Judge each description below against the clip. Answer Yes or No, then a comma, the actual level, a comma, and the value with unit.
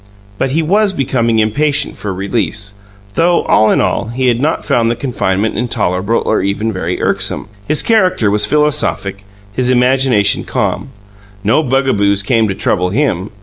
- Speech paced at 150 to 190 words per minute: Yes, average, 155 wpm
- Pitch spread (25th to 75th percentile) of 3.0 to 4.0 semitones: No, average, 5.0 semitones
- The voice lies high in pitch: No, low, 115 Hz